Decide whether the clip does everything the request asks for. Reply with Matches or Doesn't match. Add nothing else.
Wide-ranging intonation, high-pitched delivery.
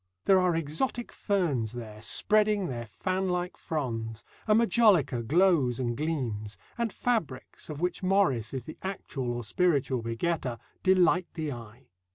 Doesn't match